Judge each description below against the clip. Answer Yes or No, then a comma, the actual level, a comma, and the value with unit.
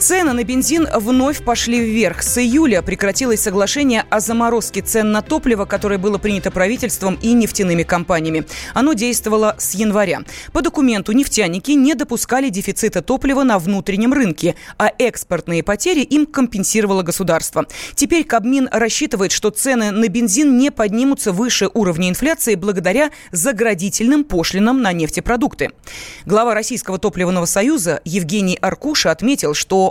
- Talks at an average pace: Yes, average, 135 wpm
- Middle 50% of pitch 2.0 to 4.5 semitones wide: No, average, 5.0 semitones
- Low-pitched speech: No, high, 220 Hz